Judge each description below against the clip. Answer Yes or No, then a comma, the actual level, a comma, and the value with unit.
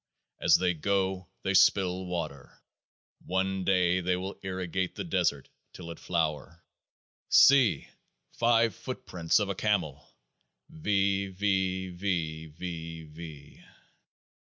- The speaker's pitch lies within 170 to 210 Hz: No, very low, 90 Hz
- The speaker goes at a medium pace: No, slow, 95 wpm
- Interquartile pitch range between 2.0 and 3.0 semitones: Yes, narrow, 2.5 semitones